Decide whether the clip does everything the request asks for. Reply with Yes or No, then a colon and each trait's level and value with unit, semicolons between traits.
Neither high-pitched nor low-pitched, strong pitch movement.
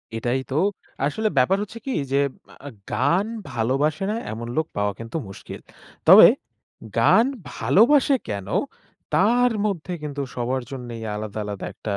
No: low, 130 Hz; wide, 9.0 semitones